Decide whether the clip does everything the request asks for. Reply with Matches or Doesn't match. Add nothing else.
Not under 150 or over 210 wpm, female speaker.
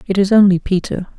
Matches